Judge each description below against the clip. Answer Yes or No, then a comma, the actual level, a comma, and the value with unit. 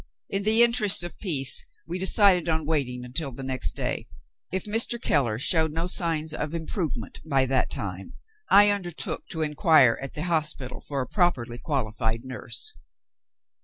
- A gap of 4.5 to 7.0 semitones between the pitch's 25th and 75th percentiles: Yes, wide, 5.5 semitones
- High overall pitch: No, medium, 155 Hz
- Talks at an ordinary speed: Yes, average, 160 wpm